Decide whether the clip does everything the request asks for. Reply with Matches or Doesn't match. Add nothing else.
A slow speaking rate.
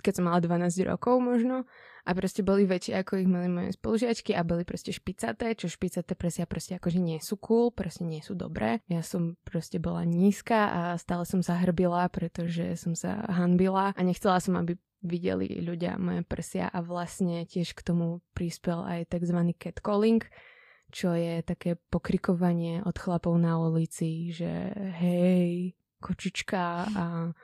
Doesn't match